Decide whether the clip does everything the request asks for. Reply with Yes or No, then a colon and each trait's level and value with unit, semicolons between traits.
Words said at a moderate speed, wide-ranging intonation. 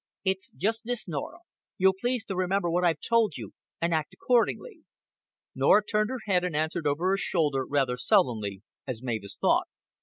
Yes: average, 175 wpm; wide, 6.8 semitones